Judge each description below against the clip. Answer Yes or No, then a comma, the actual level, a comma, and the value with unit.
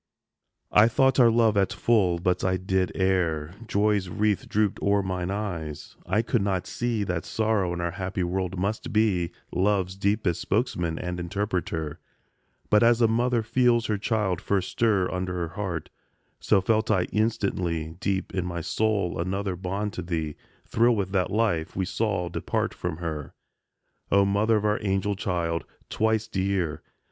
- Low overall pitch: Yes, very low, 95 Hz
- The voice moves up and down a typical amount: Yes, average, 3.2 semitones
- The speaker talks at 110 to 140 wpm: No, average, 165 wpm